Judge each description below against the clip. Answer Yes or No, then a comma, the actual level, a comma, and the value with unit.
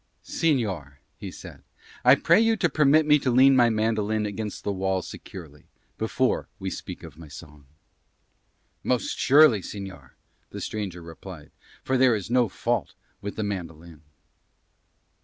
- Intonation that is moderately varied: No, wide, 6.6 semitones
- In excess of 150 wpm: No, average, 145 wpm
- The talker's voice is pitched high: No, low, 105 Hz